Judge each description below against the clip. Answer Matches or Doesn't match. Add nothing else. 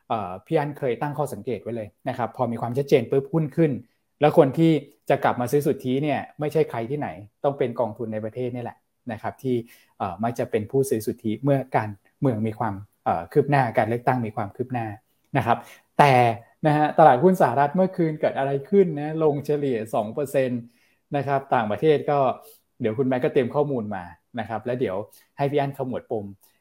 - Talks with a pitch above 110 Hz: Matches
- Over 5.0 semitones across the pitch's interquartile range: Doesn't match